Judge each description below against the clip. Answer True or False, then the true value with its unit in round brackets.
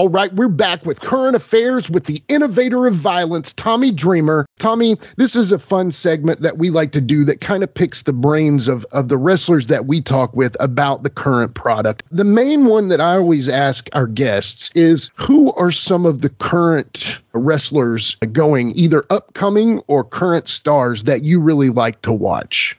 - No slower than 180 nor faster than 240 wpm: True (190 wpm)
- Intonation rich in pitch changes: True (6.1 semitones)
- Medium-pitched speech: True (165 Hz)